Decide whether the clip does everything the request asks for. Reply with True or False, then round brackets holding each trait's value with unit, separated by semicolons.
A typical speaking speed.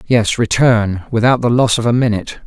True (195 wpm)